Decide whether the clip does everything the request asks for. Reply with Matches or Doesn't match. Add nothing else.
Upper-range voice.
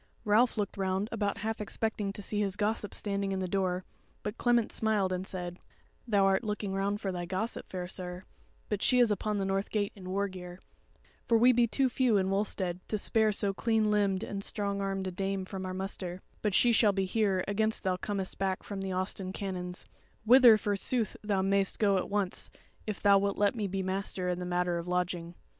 Matches